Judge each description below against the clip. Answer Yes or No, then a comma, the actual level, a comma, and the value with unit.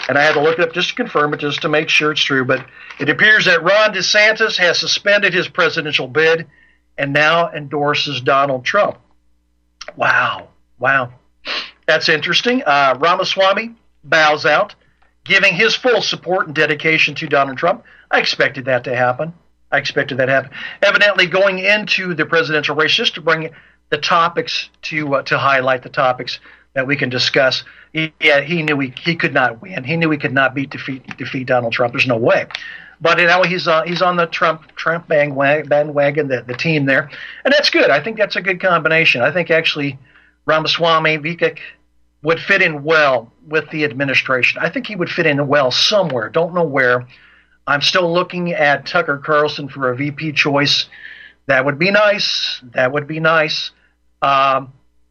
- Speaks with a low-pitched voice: No, medium, 155 Hz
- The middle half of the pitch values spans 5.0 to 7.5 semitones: No, average, 4.0 semitones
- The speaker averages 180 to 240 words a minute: Yes, average, 185 wpm